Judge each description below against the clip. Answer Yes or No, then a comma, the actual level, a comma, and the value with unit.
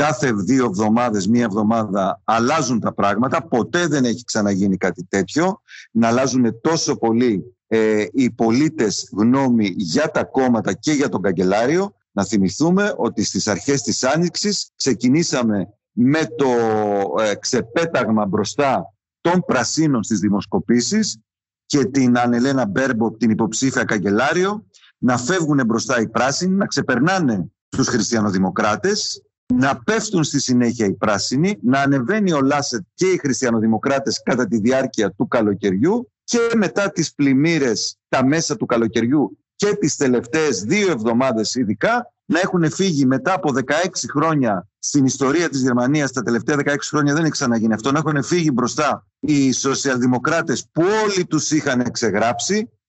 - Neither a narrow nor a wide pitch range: No, wide, 6.3 semitones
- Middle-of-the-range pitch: No, low, 130 Hz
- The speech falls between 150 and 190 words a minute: No, average, 140 wpm